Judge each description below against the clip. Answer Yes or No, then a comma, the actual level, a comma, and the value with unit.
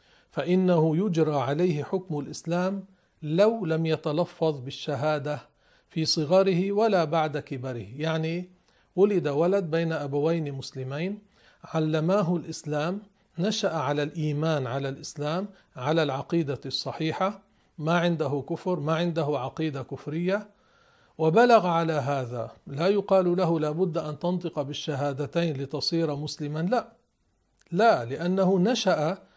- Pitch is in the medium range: Yes, medium, 160 Hz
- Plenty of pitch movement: No, average, 3.7 semitones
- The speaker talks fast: No, average, 110 wpm